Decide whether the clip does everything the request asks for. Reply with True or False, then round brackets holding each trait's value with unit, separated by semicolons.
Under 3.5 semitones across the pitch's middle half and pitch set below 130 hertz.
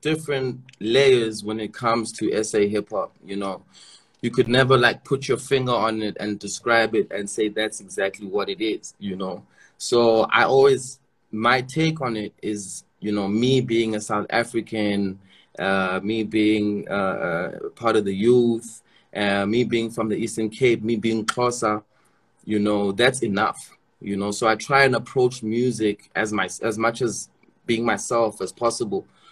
True (2.9 semitones; 115 Hz)